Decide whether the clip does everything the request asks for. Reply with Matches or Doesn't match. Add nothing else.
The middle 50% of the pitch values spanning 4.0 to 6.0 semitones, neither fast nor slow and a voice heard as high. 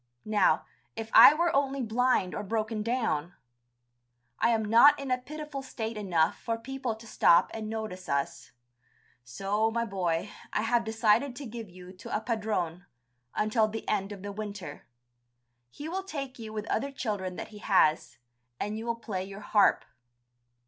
Doesn't match